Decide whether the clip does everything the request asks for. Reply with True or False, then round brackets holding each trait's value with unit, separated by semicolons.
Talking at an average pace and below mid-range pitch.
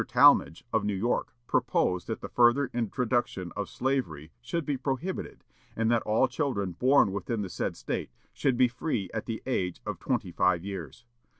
True (175 wpm; 115 Hz)